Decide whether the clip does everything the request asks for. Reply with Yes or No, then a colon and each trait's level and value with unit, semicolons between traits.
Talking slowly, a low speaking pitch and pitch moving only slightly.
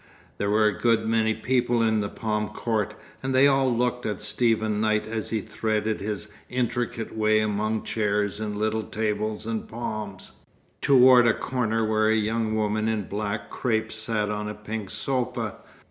No: average, 170 wpm; low, 110 Hz; narrow, 1.4 semitones